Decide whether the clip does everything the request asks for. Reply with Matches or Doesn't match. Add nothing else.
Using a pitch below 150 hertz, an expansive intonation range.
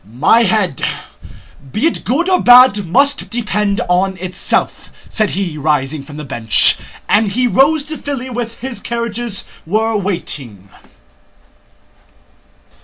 Doesn't match